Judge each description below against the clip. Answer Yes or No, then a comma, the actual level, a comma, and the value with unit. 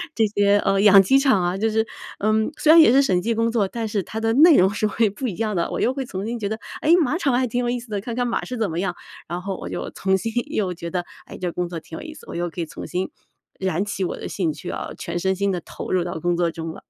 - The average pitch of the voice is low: No, high, 200 Hz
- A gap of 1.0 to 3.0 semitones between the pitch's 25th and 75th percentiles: No, average, 4.6 semitones